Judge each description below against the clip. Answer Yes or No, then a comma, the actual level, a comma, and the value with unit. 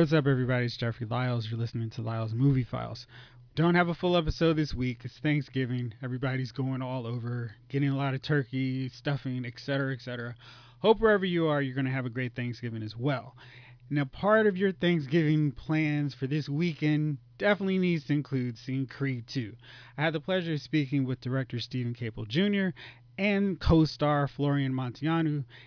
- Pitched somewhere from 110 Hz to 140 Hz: Yes, low, 135 Hz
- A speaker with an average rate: Yes, average, 180 wpm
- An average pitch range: Yes, average, 3.7 semitones